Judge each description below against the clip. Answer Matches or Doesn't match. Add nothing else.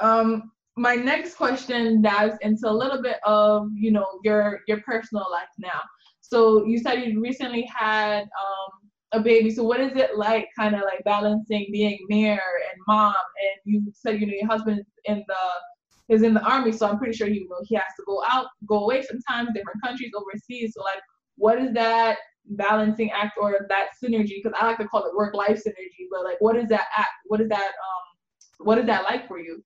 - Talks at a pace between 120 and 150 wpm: Doesn't match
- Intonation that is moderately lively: Doesn't match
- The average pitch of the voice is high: Matches